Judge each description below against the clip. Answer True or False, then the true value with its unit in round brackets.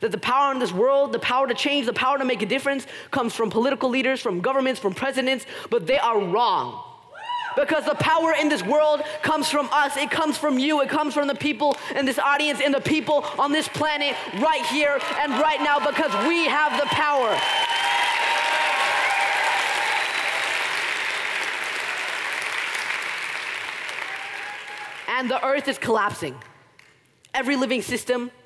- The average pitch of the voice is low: False (285 Hz)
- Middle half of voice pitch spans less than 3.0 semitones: True (2.5 semitones)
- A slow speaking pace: False (155 wpm)